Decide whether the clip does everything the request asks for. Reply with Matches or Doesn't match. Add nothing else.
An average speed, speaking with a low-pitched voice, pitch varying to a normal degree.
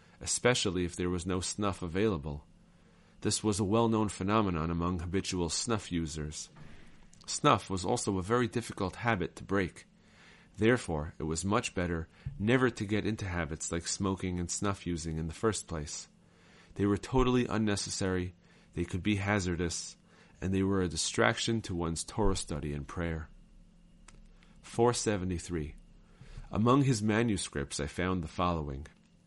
Matches